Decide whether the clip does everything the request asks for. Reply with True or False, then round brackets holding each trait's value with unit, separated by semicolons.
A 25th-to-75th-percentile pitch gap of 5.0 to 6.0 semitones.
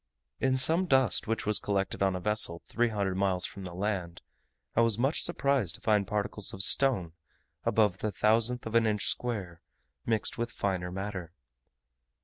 False (3.6 semitones)